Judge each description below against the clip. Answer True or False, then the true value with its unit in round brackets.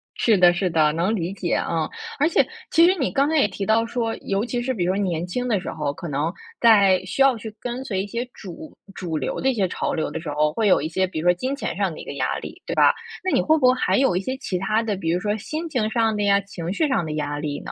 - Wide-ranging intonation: True (5.9 semitones)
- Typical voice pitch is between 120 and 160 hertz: False (200 Hz)